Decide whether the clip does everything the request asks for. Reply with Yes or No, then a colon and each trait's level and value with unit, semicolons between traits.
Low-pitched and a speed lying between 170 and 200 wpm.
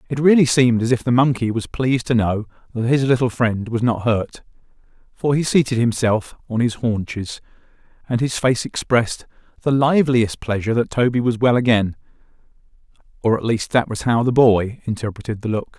Yes: low, 120 Hz; average, 180 wpm